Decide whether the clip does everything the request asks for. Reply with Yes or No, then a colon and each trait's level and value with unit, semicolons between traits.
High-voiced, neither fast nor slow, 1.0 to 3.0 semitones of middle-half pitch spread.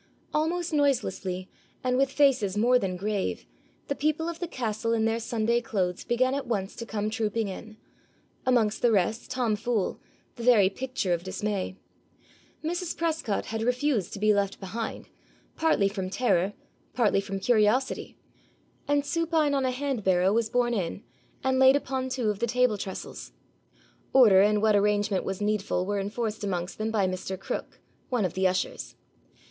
No: high, 220 Hz; average, 165 wpm; average, 4.4 semitones